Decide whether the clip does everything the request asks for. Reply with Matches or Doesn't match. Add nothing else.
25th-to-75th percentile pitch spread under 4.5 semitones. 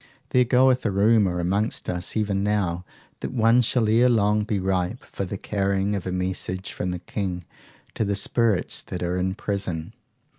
Matches